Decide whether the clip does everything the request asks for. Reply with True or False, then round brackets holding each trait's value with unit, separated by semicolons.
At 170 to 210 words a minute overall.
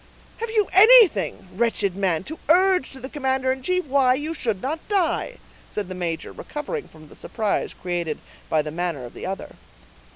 True (190 wpm)